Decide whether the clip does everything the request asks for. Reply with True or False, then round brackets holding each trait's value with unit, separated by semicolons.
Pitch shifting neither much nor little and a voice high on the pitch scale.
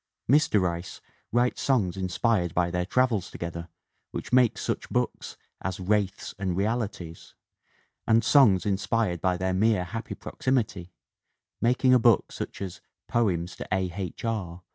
False (4.3 semitones; 95 Hz)